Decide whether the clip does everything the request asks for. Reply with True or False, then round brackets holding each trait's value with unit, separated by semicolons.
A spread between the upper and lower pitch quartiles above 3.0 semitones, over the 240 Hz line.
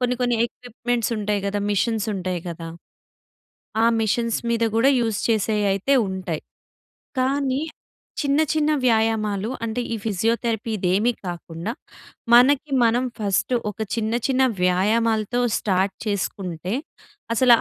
False (3.6 semitones; 220 Hz)